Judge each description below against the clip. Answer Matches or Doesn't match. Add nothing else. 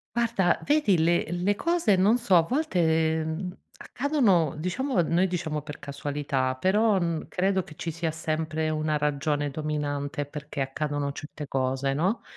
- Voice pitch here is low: Doesn't match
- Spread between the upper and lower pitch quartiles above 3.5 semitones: Matches